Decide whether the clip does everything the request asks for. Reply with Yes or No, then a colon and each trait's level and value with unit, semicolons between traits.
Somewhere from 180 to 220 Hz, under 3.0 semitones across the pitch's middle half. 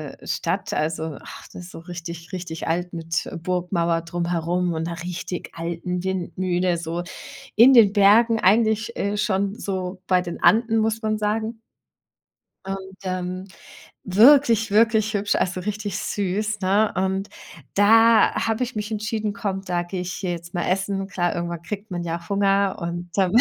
No: high, 190 Hz; average, 3.3 semitones